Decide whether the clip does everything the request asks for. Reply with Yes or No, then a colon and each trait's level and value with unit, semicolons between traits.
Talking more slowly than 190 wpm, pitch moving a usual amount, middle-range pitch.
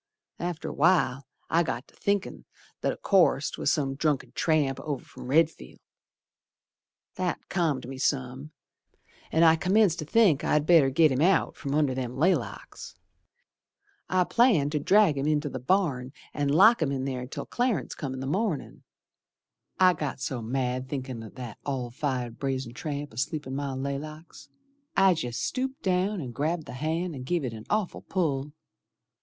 Yes: average, 170 wpm; average, 4.7 semitones; medium, 145 Hz